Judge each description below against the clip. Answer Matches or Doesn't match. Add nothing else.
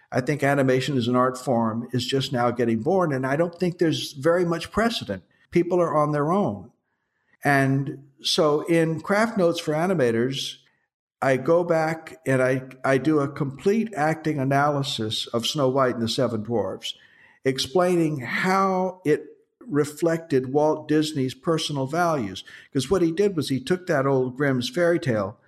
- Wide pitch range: Doesn't match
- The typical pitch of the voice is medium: Matches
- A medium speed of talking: Matches